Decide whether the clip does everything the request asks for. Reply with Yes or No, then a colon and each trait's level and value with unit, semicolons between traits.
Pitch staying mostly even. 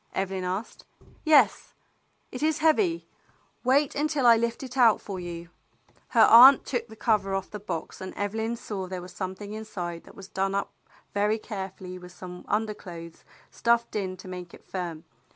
No: average, 4.2 semitones